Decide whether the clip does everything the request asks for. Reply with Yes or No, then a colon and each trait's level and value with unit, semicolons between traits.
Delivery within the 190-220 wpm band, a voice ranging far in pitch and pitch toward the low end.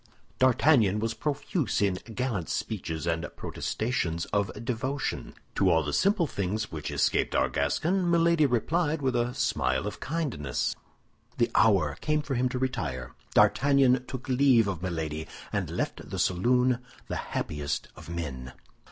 No: average, 145 wpm; wide, 8.4 semitones; low, 120 Hz